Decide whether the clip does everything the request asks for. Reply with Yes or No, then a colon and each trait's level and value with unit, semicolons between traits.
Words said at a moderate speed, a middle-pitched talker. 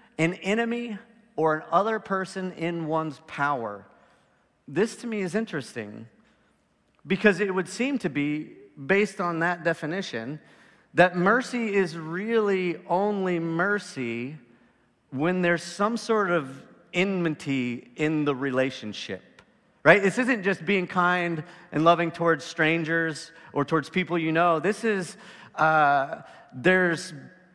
No: slow, 125 wpm; medium, 175 Hz